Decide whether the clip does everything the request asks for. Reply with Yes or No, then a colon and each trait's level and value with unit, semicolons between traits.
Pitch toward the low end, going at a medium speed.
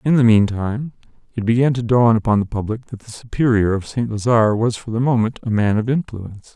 No: low, 115 Hz; fast, 220 wpm